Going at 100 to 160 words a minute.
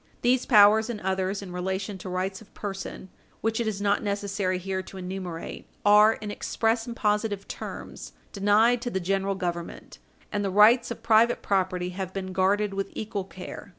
No: average, 180 wpm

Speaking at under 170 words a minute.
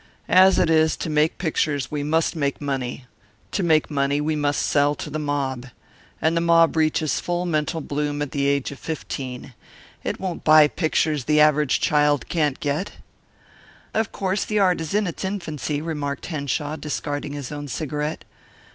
No: average, 175 wpm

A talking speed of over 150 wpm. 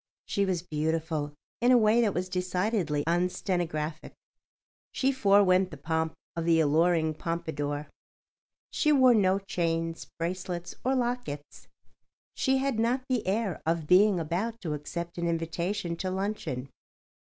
No: slow, 135 wpm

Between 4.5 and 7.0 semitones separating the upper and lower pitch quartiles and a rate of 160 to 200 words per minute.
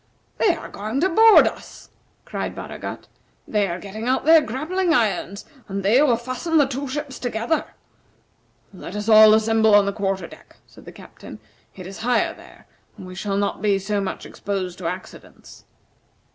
Yes: average, 5.1 semitones; average, 175 wpm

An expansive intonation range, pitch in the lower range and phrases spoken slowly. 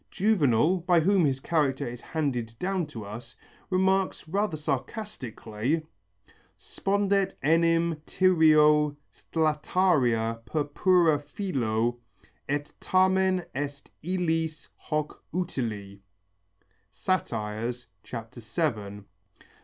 No: wide, 7.0 semitones; medium, 150 Hz; slow, 85 wpm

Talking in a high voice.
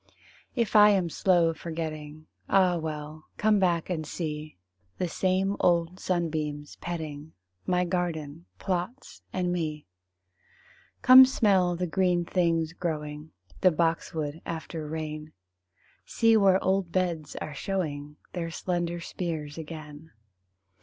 No: medium, 170 Hz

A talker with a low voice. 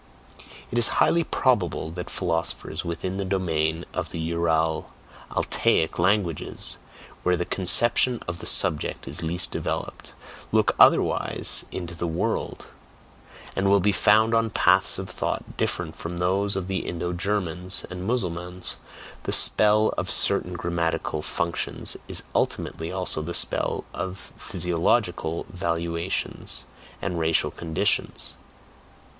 Yes: very low, 90 Hz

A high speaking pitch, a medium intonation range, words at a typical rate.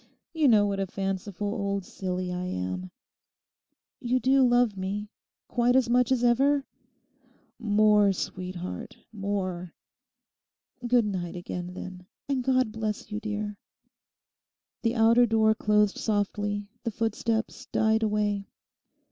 No: high, 210 Hz; average, 3.1 semitones; slow, 120 wpm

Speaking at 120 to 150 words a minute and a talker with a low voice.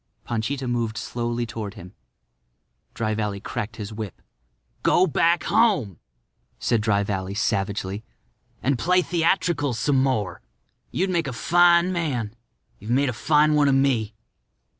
Yes: average, 140 wpm; low, 120 Hz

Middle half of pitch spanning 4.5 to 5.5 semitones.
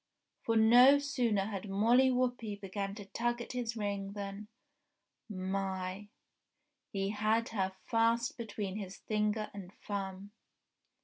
No: average, 2.8 semitones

